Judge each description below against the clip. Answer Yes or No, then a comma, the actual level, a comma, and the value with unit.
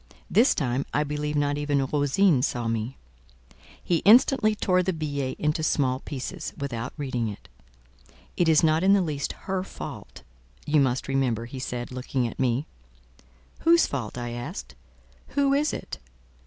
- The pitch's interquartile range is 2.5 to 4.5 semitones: No, average, 5.1 semitones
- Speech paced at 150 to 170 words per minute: Yes, average, 155 wpm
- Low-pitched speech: No, medium, 145 Hz